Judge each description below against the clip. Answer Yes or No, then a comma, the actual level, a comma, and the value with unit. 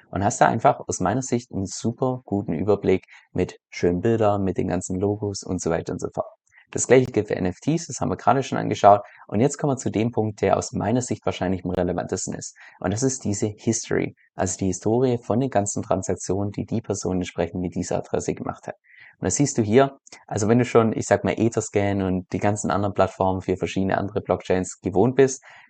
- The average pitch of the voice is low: Yes, low, 100 Hz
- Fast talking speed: Yes, fast, 220 wpm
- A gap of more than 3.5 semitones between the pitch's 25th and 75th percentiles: Yes, average, 4.2 semitones